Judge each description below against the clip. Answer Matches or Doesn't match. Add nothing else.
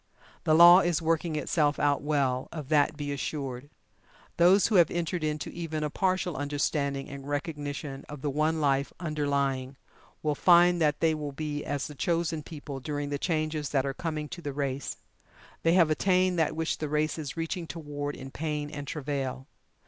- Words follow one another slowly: Doesn't match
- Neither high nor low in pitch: Matches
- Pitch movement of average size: Doesn't match